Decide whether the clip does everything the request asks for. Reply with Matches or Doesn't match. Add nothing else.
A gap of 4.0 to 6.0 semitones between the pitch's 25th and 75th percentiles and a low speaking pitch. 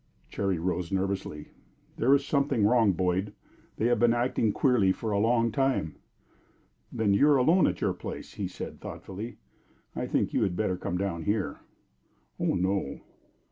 Matches